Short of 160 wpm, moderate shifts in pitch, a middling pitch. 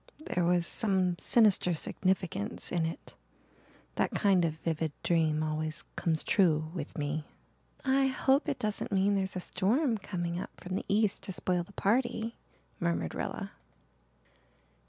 Yes: average, 145 wpm; average, 4.0 semitones; medium, 180 Hz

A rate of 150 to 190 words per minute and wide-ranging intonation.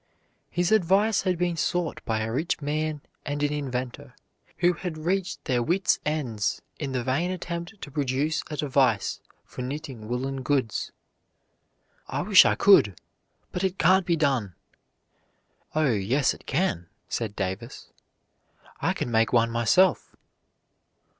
No: average, 140 wpm; wide, 6.1 semitones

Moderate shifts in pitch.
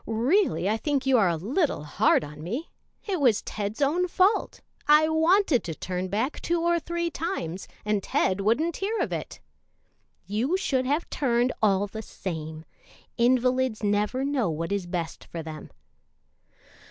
No: wide, 8.4 semitones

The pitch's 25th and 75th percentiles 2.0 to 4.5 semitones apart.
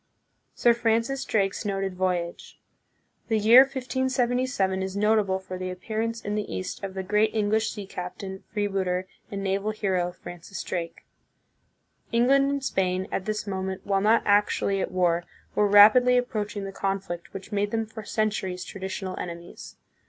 Yes: average, 2.7 semitones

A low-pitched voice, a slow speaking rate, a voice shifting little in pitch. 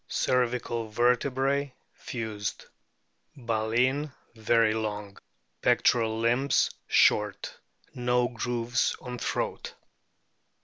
Yes: low, 120 Hz; slow, 75 wpm; narrow, 2.1 semitones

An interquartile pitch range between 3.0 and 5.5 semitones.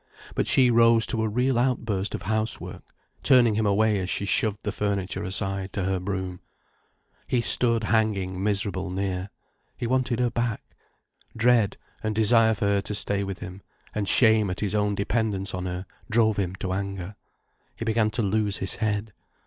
No: narrow, 2.5 semitones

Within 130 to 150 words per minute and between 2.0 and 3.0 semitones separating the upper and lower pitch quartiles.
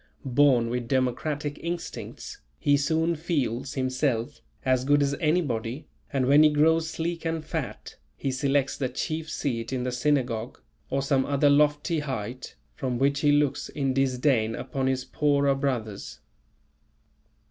Yes: average, 145 wpm; narrow, 2.6 semitones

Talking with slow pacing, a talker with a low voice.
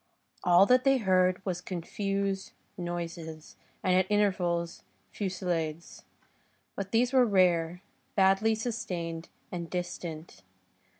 No: slow, 105 wpm; medium, 185 Hz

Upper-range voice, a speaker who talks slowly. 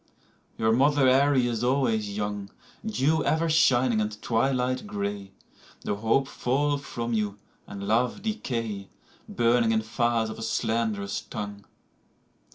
No: low, 115 Hz; slow, 130 wpm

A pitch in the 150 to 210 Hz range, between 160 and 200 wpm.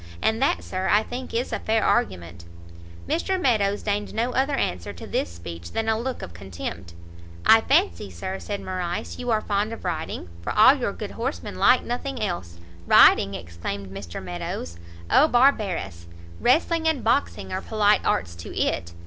Yes: high, 190 Hz; average, 175 wpm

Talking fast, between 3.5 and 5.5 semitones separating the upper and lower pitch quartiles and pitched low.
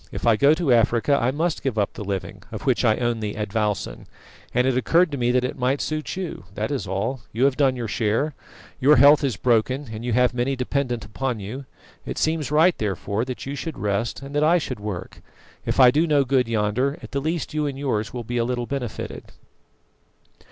Yes: fast, 220 wpm; average, 4.1 semitones; low, 125 Hz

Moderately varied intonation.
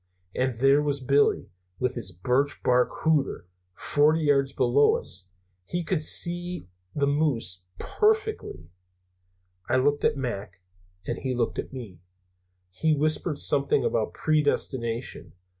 Yes: average, 4.1 semitones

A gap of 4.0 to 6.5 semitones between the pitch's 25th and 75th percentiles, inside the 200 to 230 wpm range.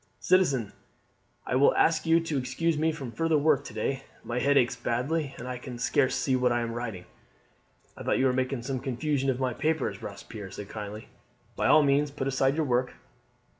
No: average, 3.2 semitones; fast, 205 wpm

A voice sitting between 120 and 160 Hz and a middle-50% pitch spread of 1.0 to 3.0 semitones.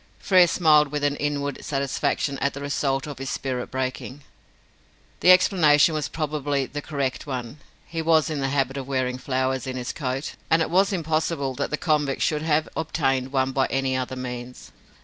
Yes: medium, 140 Hz; average, 2.7 semitones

